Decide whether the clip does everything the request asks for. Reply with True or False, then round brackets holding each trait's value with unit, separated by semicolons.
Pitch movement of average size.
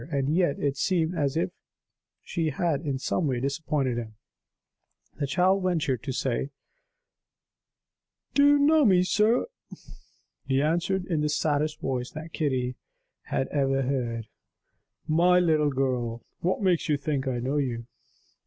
True (4.6 semitones)